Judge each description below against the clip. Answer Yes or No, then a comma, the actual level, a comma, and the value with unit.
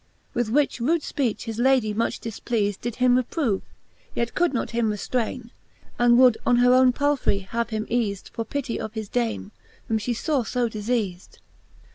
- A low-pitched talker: No, high, 235 Hz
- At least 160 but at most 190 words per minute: Yes, average, 175 wpm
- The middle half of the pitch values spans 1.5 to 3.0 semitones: Yes, narrow, 2.5 semitones